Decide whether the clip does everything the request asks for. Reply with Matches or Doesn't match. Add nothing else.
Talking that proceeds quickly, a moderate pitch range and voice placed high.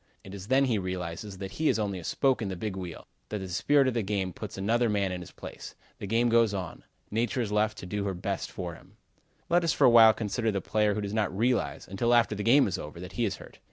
Doesn't match